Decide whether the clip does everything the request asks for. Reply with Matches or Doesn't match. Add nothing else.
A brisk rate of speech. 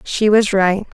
Doesn't match